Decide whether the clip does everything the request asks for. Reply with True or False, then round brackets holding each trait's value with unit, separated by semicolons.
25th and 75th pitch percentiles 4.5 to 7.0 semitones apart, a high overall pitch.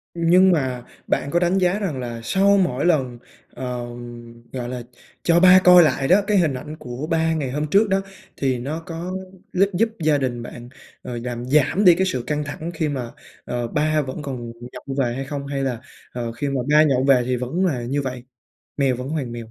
False (5.1 semitones; 140 Hz)